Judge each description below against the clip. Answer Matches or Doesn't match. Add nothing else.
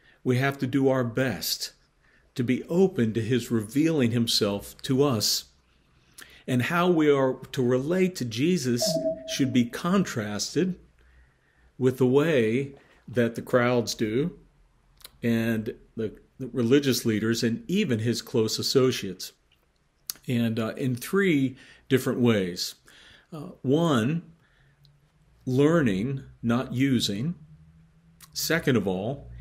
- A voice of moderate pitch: Doesn't match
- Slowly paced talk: Matches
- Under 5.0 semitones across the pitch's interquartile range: Matches